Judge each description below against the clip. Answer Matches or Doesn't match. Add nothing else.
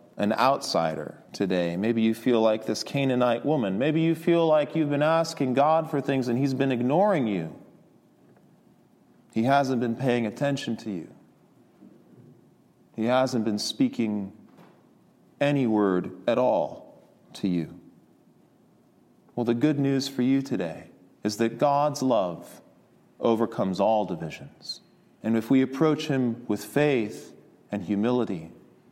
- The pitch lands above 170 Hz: Doesn't match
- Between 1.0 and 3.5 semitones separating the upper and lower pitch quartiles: Doesn't match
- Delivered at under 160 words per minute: Matches